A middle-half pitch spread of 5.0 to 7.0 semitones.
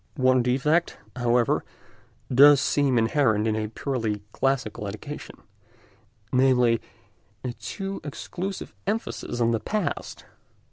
No: average, 4.1 semitones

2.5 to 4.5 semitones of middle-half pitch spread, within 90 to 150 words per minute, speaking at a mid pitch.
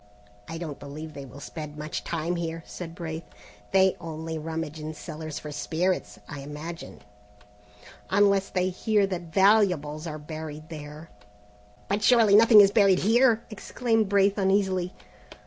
Yes: average, 4.2 semitones; average, 145 wpm; medium, 170 Hz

